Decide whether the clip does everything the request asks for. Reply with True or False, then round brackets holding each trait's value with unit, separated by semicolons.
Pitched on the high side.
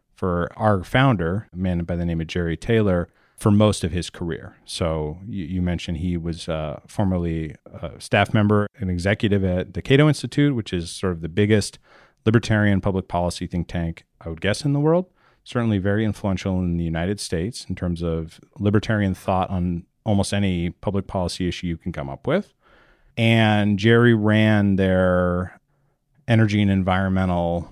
False (95 Hz)